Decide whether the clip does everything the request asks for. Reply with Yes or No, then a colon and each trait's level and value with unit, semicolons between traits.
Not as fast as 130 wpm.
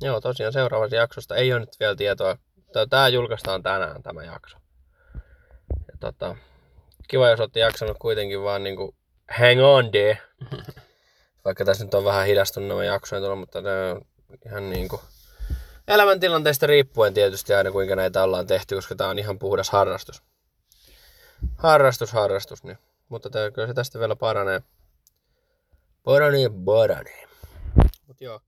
No: average, 145 wpm